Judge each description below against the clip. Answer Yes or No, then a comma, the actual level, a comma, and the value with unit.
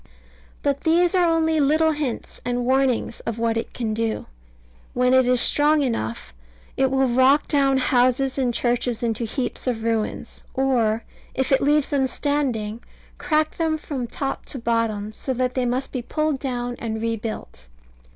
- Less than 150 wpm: No, average, 165 wpm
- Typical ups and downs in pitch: Yes, average, 3.5 semitones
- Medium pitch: No, very high, 255 Hz